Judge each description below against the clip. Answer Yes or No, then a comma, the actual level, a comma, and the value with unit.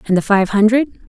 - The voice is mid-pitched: No, high, 215 Hz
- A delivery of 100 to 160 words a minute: No, fast, 205 wpm